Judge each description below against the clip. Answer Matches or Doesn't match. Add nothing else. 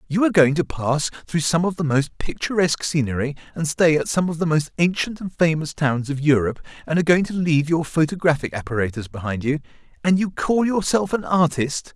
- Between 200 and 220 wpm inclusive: Matches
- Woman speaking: Doesn't match